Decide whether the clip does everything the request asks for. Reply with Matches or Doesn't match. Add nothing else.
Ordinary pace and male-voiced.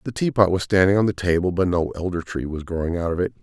Doesn't match